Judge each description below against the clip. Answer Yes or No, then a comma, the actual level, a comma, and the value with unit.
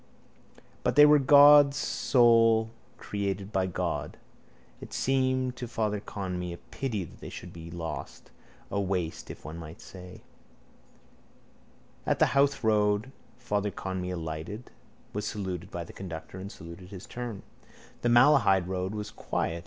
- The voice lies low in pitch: Yes, low, 100 Hz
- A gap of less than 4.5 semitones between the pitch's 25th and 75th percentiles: No, average, 5.0 semitones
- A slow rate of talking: No, average, 155 wpm